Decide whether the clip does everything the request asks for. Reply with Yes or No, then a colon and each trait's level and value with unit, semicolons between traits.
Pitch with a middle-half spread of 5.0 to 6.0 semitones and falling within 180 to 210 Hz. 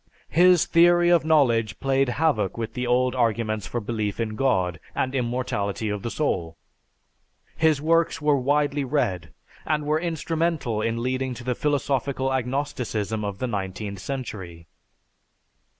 No: average, 5.3 semitones; low, 125 Hz